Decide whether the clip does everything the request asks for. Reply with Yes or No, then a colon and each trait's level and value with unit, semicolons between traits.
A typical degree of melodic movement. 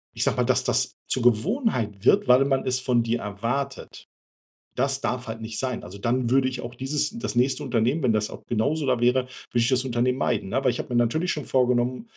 No: narrow, 2.3 semitones